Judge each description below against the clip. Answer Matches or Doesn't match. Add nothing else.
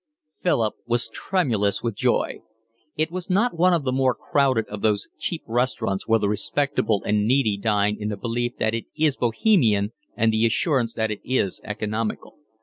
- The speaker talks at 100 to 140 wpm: Doesn't match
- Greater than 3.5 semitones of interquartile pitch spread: Matches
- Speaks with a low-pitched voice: Matches